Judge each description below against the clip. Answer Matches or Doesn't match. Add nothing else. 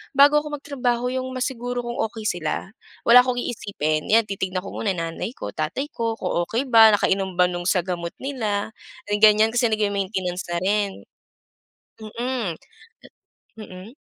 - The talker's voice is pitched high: Matches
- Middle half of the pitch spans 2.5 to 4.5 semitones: Doesn't match